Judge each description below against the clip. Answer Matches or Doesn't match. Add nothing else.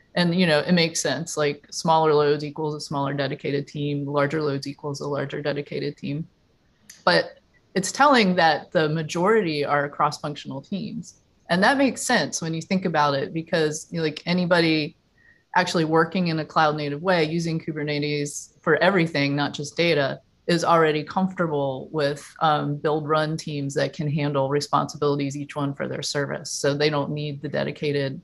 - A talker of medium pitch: Matches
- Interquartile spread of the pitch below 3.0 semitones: Matches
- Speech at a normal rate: Matches